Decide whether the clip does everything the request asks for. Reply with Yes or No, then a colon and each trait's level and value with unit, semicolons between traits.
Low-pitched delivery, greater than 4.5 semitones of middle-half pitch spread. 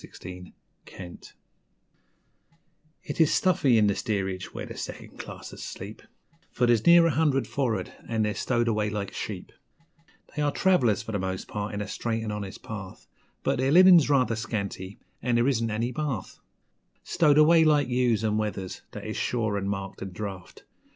Yes: low, 110 Hz; average, 5.1 semitones